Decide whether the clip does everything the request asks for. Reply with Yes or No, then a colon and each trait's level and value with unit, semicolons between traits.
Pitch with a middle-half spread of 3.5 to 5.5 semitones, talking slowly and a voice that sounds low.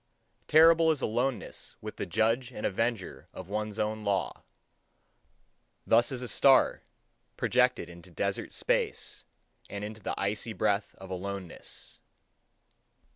Yes: average, 3.8 semitones; slow, 125 wpm; low, 110 Hz